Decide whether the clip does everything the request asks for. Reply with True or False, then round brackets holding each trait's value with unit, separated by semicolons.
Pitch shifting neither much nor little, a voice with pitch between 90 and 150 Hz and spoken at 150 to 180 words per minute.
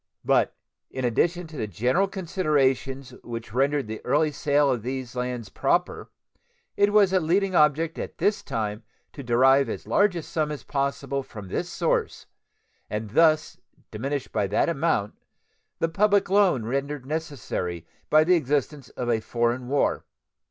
True (5.0 semitones; 140 Hz; 155 wpm)